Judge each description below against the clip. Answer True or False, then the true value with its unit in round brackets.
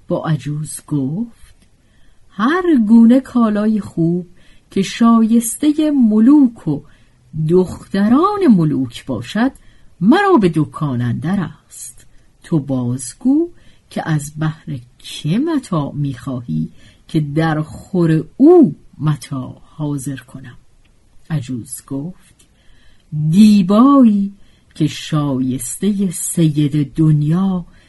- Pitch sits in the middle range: True (160 Hz)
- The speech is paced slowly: True (85 wpm)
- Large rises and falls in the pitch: True (7.7 semitones)